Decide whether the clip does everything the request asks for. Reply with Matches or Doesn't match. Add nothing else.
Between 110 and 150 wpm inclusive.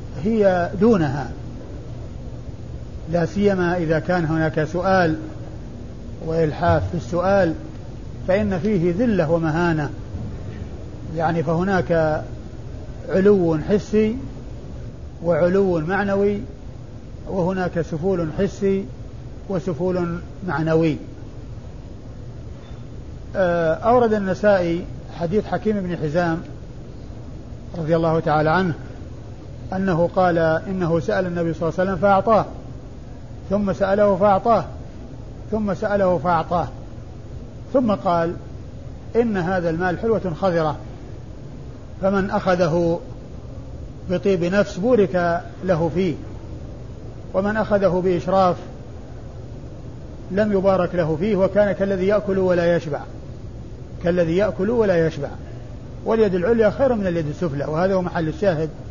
Doesn't match